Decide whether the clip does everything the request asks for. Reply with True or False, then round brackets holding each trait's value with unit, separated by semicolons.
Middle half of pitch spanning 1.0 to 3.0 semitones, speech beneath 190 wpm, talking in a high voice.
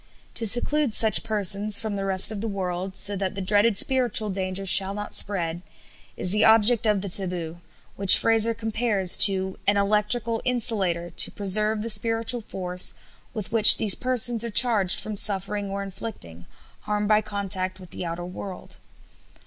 True (2.7 semitones; 165 wpm; 205 Hz)